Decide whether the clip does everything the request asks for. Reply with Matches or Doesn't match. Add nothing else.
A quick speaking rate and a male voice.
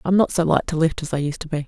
Doesn't match